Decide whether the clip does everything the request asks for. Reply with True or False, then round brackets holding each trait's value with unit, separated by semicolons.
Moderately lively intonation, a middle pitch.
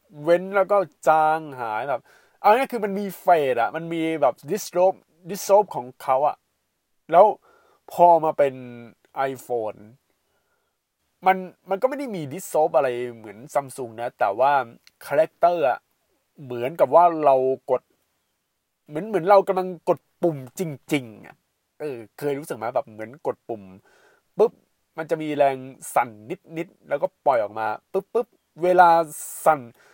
False (6.3 semitones; 160 Hz)